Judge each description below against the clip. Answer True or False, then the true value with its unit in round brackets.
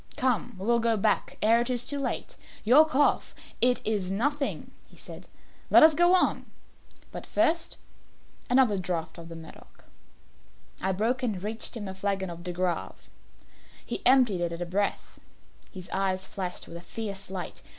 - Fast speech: False (175 wpm)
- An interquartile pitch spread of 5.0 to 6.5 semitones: True (5.4 semitones)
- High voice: True (210 Hz)